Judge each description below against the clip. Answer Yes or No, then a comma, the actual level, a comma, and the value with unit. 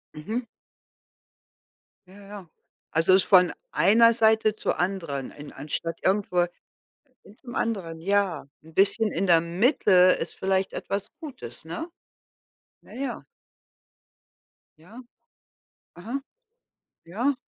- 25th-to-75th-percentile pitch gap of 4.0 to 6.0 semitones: Yes, average, 4.5 semitones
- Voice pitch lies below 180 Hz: No, high, 195 Hz